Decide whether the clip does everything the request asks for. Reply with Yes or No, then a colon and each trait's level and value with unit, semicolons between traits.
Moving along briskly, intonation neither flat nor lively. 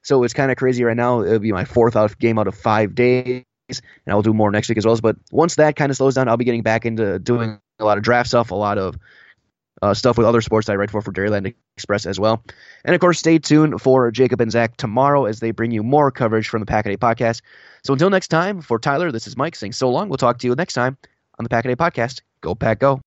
Yes: fast, 275 wpm; average, 3.3 semitones